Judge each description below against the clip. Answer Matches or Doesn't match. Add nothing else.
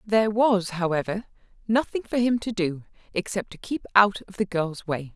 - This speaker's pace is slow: Doesn't match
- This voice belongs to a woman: Matches